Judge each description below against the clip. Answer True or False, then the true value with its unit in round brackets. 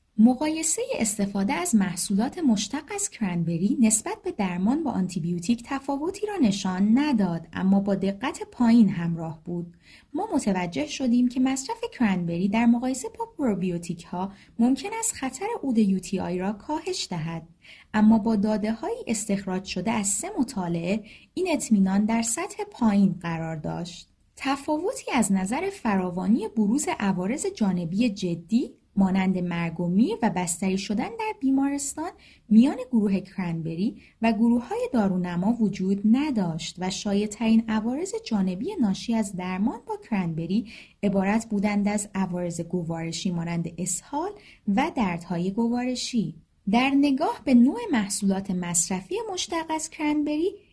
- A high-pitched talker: True (220 Hz)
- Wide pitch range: True (6.1 semitones)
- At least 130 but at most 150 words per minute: True (135 wpm)